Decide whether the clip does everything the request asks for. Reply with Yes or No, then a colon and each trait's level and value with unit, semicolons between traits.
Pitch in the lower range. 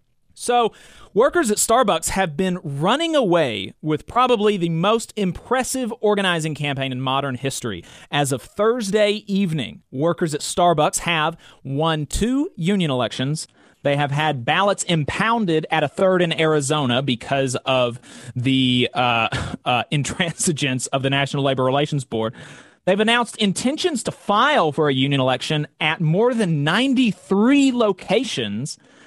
No: medium, 160 Hz